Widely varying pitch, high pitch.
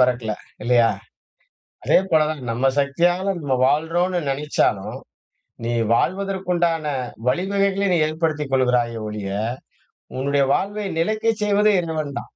No: wide, 6.3 semitones; medium, 155 Hz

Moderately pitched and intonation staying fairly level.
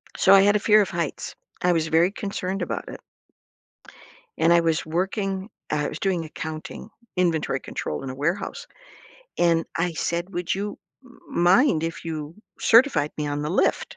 No: medium, 175 Hz; average, 3.6 semitones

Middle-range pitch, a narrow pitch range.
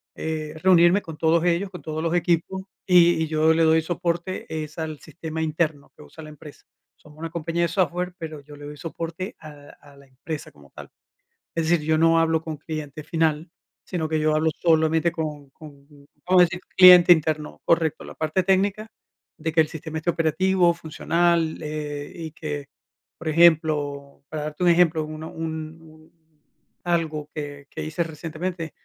Yes: medium, 160 Hz; narrow, 1.9 semitones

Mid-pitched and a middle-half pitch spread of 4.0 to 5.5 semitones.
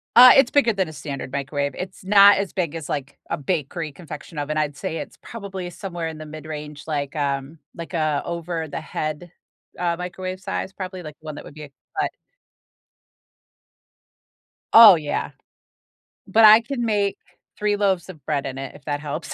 Yes: medium, 165 Hz; average, 4.4 semitones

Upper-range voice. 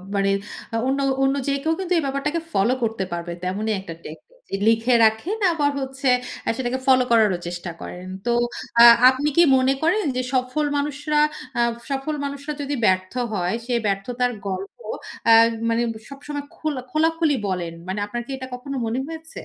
Yes: very high, 255 Hz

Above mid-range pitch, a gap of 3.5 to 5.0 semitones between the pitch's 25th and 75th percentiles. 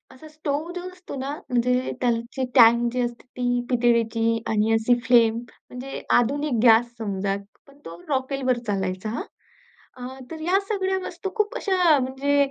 Yes: very high, 250 Hz; average, 3.8 semitones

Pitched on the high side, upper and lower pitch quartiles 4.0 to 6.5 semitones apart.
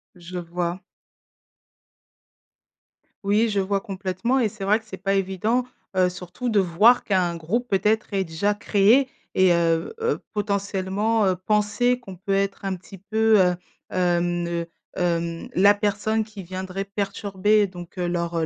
No: high, 195 Hz; average, 2.8 semitones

